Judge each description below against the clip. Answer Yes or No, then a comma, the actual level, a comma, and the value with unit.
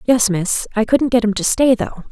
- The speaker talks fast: Yes, fast, 255 wpm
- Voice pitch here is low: No, high, 225 Hz